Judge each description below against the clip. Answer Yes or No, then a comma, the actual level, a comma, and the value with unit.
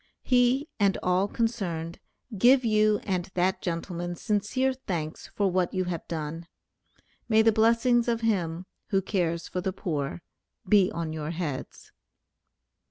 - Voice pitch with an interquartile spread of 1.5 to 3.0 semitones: No, average, 4.7 semitones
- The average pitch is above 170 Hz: Yes, medium, 185 Hz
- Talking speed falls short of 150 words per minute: Yes, average, 140 wpm